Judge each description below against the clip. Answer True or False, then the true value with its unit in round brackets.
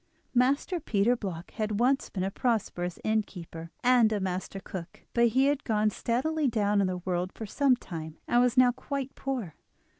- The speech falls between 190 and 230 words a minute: False (180 wpm)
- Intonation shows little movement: False (5.0 semitones)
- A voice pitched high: True (220 Hz)